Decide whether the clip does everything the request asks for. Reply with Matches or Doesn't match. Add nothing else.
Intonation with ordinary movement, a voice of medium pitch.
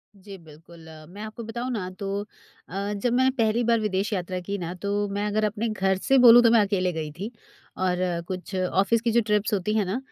Doesn't match